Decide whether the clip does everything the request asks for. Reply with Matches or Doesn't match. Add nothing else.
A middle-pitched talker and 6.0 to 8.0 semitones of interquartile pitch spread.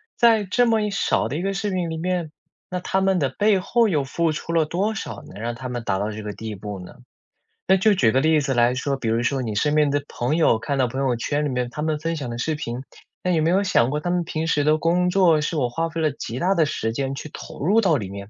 Matches